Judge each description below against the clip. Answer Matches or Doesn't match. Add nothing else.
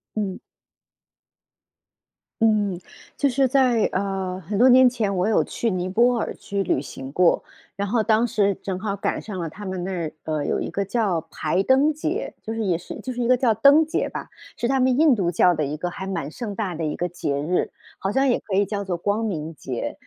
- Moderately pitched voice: Doesn't match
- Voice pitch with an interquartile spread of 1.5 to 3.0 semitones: Doesn't match